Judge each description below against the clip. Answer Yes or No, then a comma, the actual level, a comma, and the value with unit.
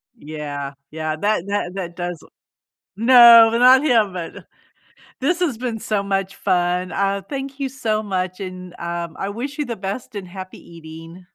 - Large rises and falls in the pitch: No, average, 4.9 semitones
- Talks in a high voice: Yes, high, 195 Hz